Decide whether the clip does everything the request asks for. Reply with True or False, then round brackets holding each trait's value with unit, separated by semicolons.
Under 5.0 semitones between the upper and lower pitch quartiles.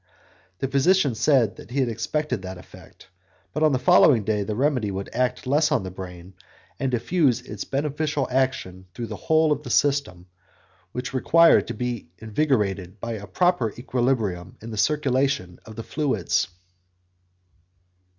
False (5.6 semitones)